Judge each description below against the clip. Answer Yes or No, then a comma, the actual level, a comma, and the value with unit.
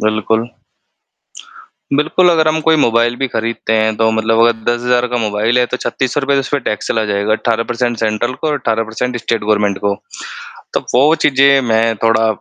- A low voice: Yes, low, 115 Hz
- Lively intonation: No, average, 2.7 semitones